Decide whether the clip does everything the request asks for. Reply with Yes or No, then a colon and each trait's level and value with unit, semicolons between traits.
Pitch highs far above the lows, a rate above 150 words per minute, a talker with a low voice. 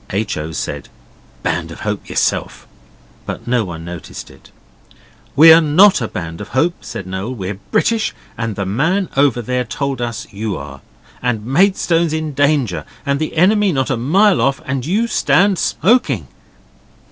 Yes: wide, 7.8 semitones; average, 160 wpm; low, 130 Hz